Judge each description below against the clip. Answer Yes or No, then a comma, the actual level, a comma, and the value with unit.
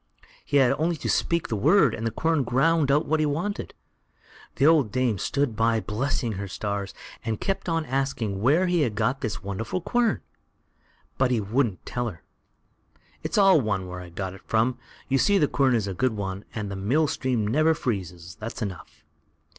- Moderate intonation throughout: No, wide, 6.4 semitones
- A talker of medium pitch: No, low, 120 Hz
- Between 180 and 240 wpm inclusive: Yes, average, 195 wpm